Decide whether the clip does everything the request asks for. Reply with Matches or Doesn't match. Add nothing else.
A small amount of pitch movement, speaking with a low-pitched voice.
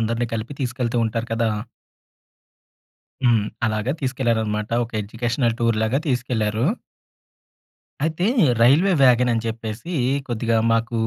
Matches